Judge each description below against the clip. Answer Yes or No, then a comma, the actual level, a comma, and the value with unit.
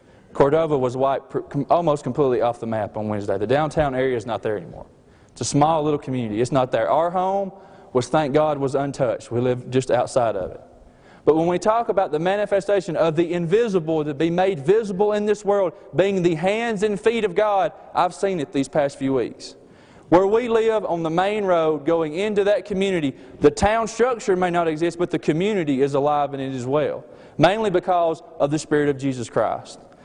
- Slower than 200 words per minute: No, fast, 205 wpm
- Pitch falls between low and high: Yes, medium, 165 Hz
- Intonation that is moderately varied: No, wide, 5.8 semitones